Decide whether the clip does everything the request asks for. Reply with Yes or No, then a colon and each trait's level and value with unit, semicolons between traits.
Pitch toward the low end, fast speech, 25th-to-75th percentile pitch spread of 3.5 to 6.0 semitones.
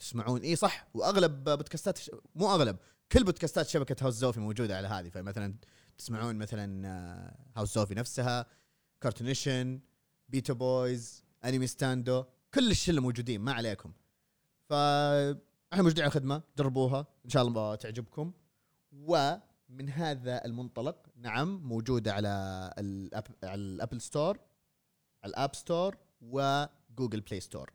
No: low, 130 Hz; average, 120 wpm; average, 4.5 semitones